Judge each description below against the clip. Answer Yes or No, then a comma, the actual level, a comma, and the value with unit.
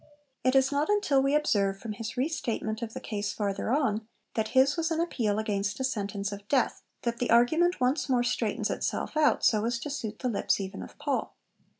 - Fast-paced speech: Yes, fast, 215 wpm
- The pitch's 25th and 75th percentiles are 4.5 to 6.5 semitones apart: Yes, average, 4.9 semitones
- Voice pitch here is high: Yes, high, 240 Hz